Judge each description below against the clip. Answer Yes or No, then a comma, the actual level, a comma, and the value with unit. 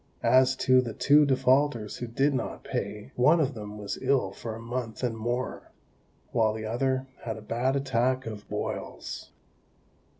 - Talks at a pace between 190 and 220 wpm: No, average, 165 wpm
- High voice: No, low, 120 Hz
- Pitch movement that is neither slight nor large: Yes, average, 3.0 semitones